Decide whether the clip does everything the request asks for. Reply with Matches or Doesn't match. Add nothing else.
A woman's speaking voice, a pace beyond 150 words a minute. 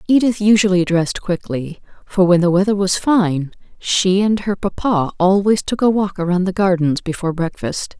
Matches